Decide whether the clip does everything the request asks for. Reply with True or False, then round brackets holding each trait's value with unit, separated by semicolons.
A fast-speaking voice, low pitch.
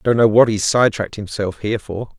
True (245 wpm; 105 Hz)